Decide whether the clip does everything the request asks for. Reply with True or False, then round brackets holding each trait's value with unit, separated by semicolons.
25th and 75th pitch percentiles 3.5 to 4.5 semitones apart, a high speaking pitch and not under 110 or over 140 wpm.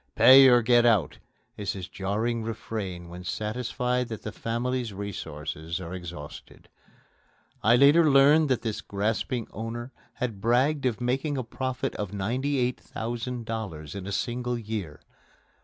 False (3.9 semitones; 115 Hz; 135 wpm)